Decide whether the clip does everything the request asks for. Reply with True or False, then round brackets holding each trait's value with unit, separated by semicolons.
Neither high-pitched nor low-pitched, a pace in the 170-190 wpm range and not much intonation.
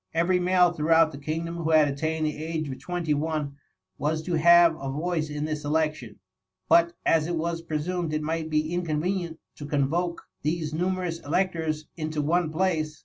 True (160 Hz; 175 wpm; 2.0 semitones)